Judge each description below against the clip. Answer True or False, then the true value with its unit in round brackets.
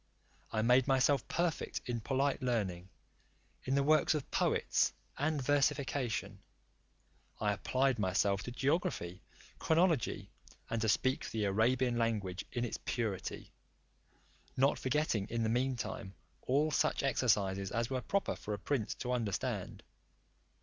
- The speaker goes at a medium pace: False (130 wpm)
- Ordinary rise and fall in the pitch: True (4.4 semitones)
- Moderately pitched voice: False (125 Hz)